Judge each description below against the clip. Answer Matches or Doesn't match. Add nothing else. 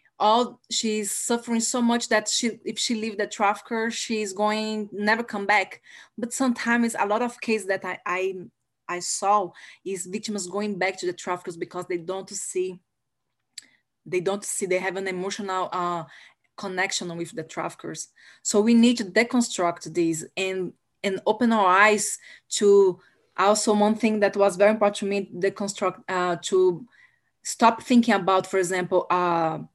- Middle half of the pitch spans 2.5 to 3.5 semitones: Matches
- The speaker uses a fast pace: Doesn't match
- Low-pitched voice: Doesn't match